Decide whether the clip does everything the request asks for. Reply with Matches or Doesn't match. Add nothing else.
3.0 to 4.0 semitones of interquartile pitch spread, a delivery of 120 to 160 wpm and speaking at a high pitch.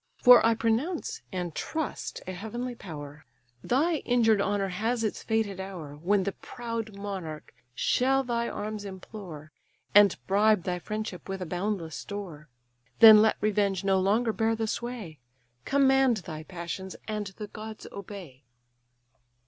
Matches